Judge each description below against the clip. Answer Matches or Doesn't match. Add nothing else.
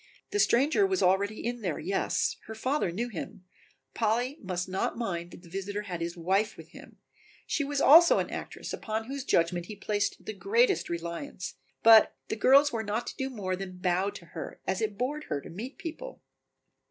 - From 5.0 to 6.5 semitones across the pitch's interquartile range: Matches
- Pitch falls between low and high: Doesn't match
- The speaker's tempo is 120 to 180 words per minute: Doesn't match